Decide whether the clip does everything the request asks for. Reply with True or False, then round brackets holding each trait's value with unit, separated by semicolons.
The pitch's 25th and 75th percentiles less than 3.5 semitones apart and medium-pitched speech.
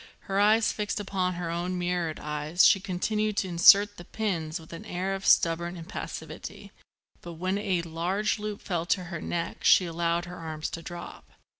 True (2.7 semitones; 180 Hz)